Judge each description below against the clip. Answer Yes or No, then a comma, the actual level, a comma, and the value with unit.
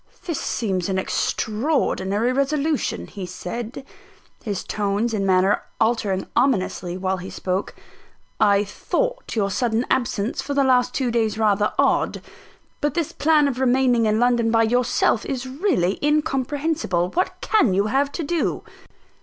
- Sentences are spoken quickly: No, average, 145 wpm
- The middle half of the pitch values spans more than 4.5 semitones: Yes, wide, 5.5 semitones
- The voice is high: Yes, high, 235 Hz